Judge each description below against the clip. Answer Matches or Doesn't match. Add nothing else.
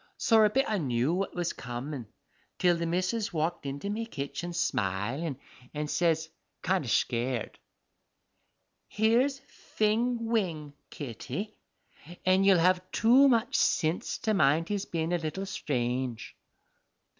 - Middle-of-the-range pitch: Matches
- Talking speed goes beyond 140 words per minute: Doesn't match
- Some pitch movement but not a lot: Doesn't match